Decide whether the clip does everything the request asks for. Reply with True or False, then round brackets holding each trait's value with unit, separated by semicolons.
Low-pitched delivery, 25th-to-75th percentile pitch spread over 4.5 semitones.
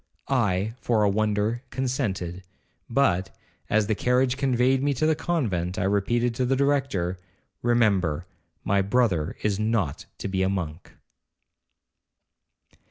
True (110 Hz; 4.9 semitones)